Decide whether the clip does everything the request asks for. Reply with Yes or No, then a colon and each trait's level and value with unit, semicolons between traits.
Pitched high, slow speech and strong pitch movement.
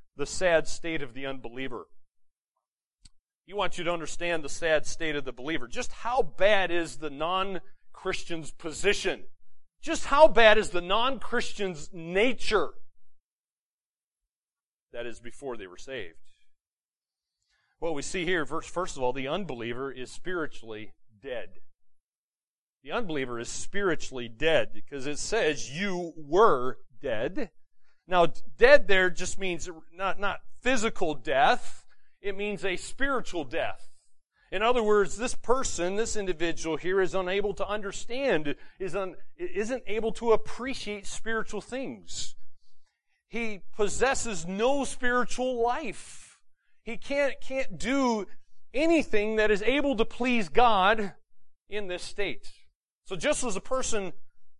Yes: high, 195 Hz; slow, 130 wpm; wide, 6.4 semitones